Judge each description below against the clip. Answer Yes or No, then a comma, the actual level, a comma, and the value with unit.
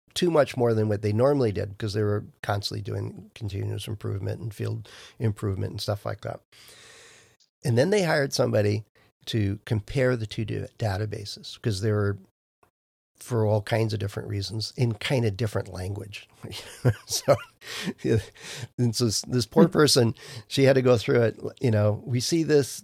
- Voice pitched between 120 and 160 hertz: No, low, 110 Hz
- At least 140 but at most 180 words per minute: Yes, average, 170 wpm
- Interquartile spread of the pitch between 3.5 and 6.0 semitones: No, average, 3.0 semitones